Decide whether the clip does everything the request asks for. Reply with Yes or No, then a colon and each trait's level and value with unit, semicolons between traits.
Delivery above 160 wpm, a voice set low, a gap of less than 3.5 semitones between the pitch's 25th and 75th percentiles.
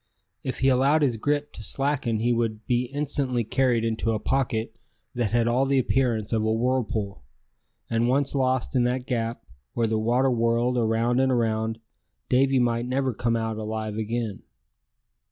Yes: average, 170 wpm; low, 120 Hz; narrow, 2.6 semitones